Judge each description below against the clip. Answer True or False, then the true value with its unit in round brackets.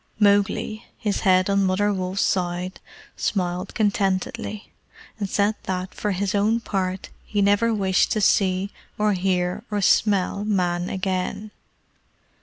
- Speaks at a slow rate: True (130 wpm)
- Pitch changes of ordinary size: False (1.9 semitones)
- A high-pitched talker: True (195 Hz)